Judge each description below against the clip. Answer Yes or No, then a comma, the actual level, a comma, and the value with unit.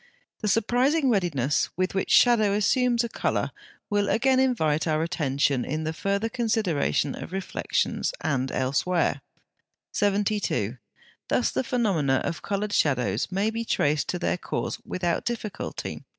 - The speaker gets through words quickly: No, slow, 135 wpm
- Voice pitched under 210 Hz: Yes, high, 190 Hz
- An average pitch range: No, wide, 6.9 semitones